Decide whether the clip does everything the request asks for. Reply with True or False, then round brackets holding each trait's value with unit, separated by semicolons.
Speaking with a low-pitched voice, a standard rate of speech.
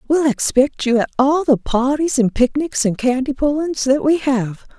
False (270 Hz; 190 wpm)